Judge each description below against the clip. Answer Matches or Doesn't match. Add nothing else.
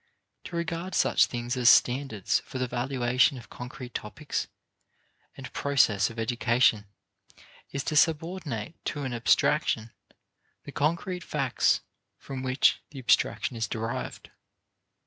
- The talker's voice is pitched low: Matches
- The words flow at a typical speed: Doesn't match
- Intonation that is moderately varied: Matches